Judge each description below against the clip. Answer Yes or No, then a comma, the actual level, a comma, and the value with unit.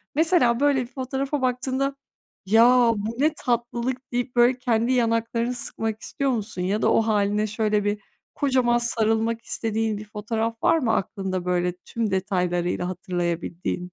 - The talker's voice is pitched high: Yes, high, 230 Hz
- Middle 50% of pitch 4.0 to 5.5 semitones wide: No, average, 3.2 semitones